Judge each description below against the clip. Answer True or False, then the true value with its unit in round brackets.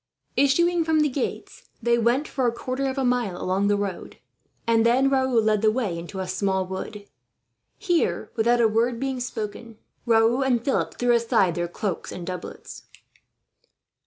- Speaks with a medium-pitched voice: False (235 Hz)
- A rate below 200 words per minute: True (170 wpm)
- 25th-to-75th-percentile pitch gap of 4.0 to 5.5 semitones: True (4.3 semitones)